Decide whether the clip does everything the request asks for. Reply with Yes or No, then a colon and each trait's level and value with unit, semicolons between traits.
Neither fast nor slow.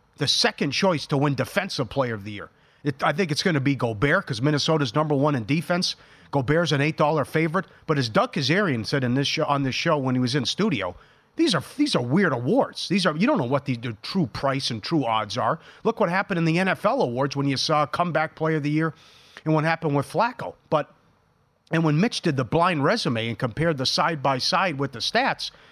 No: fast, 235 wpm